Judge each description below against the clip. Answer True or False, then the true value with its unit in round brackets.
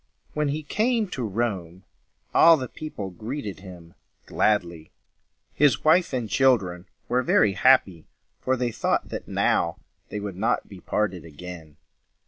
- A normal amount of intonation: False (6.8 semitones)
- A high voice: False (105 Hz)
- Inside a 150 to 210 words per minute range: False (140 wpm)